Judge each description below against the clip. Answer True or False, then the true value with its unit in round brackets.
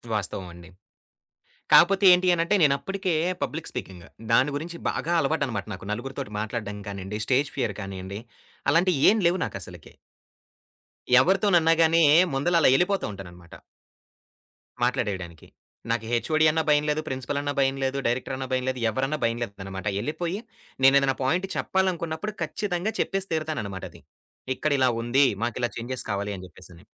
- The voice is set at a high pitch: False (135 Hz)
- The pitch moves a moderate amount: False (7.9 semitones)